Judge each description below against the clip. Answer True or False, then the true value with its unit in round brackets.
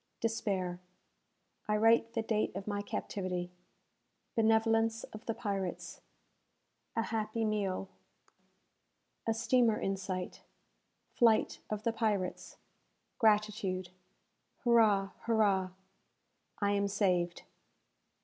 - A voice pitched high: True (210 Hz)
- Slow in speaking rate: True (95 wpm)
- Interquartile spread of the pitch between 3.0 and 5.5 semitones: False (2.5 semitones)